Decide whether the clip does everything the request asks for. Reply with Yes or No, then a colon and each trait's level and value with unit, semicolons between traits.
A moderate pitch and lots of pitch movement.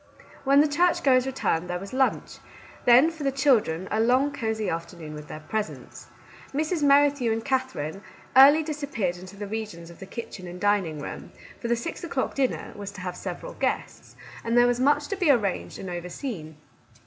No: high, 230 Hz; wide, 7.3 semitones